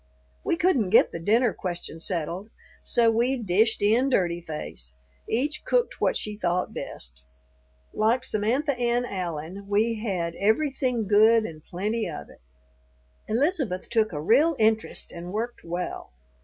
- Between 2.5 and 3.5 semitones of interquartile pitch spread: No, average, 5.3 semitones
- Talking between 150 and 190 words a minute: No, average, 140 wpm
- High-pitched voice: Yes, high, 215 Hz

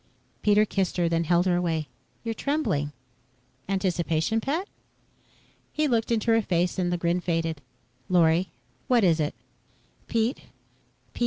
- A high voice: No, medium, 180 Hz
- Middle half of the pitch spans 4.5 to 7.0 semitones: Yes, average, 5.1 semitones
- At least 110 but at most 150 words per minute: Yes, average, 140 wpm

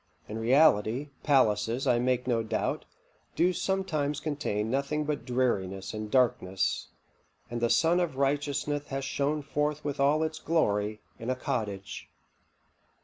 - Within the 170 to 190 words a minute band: No, average, 140 wpm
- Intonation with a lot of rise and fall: No, average, 4.8 semitones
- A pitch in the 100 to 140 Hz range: Yes, low, 135 Hz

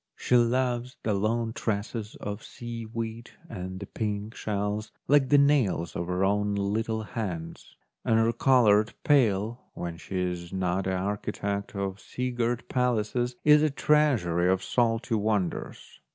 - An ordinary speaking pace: Yes, average, 150 wpm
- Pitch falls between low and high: No, low, 110 Hz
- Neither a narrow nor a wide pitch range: Yes, average, 3.5 semitones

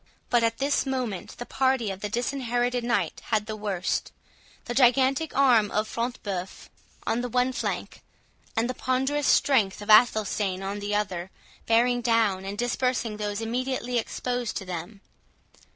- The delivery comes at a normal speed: Yes, average, 160 wpm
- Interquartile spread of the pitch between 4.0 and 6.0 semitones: No, average, 3.3 semitones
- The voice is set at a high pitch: Yes, high, 230 Hz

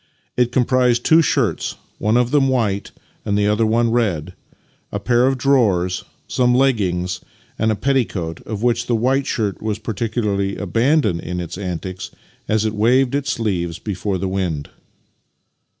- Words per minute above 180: No, average, 160 wpm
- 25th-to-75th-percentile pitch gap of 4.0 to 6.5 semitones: Yes, average, 4.3 semitones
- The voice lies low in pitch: Yes, low, 110 Hz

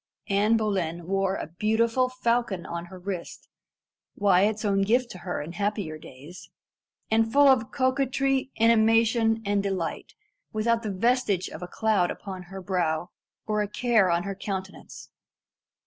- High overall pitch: Yes, high, 205 Hz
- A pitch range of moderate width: Yes, average, 3.7 semitones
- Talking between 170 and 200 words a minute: No, average, 150 wpm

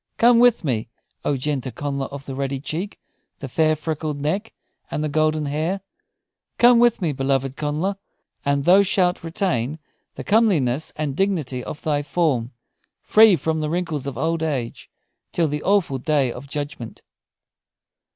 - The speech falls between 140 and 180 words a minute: Yes, average, 155 wpm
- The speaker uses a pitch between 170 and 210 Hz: No, medium, 150 Hz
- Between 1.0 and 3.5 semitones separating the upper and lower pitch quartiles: No, average, 4.2 semitones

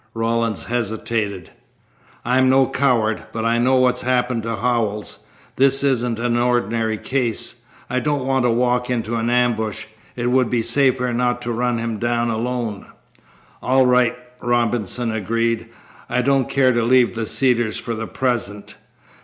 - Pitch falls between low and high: No, low, 120 Hz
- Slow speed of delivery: No, average, 155 wpm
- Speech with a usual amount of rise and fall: No, narrow, 1.7 semitones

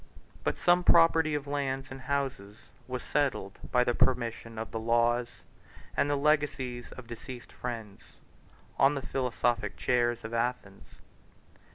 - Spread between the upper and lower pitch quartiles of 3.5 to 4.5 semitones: No, average, 3.1 semitones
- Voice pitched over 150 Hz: No, low, 125 Hz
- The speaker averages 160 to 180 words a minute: No, average, 140 wpm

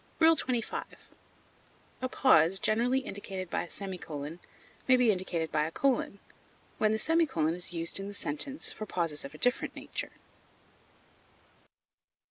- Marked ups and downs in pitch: Yes, wide, 7.1 semitones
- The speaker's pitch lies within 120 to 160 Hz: No, high, 195 Hz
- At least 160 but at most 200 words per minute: No, slow, 135 wpm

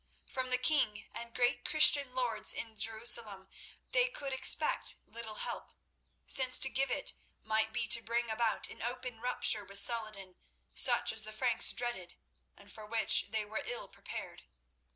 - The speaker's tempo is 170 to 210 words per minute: No, average, 160 wpm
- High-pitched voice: Yes, high, 230 Hz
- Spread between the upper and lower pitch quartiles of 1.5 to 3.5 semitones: Yes, average, 2.7 semitones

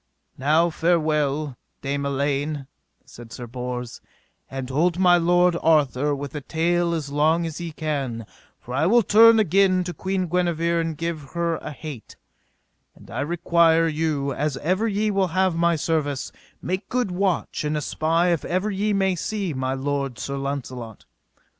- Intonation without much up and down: No, average, 3.9 semitones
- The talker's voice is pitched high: No, medium, 160 Hz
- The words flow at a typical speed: Yes, average, 160 wpm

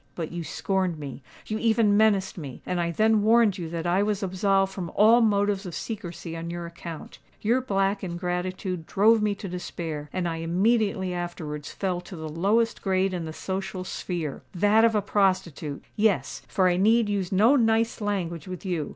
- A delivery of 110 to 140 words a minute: No, average, 175 wpm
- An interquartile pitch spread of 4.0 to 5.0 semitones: No, average, 3.3 semitones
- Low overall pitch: No, high, 190 Hz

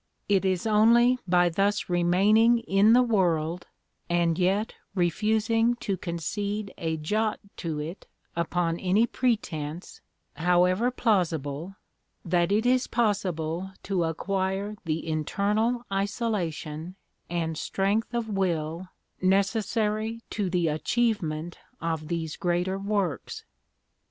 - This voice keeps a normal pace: No, slow, 110 wpm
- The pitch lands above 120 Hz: Yes, high, 190 Hz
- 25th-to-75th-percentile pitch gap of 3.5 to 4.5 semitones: Yes, average, 4.2 semitones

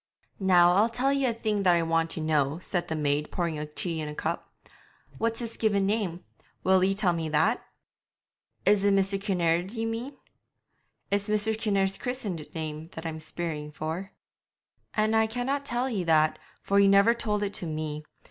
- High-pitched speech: Yes, high, 195 Hz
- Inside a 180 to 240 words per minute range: Yes, average, 185 wpm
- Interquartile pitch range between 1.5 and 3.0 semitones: No, average, 5.1 semitones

